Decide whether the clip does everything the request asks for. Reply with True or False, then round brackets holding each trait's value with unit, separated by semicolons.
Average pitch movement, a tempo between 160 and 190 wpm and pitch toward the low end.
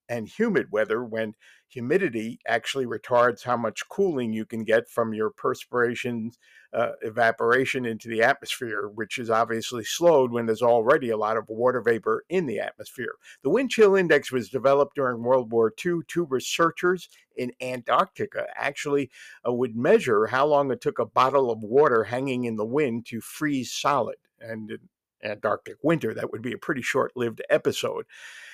True (3.4 semitones; 170 wpm; 120 Hz)